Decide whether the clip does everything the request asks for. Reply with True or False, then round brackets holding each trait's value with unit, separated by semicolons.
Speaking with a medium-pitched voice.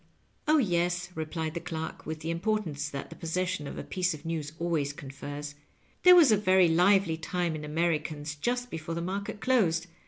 True (165 Hz)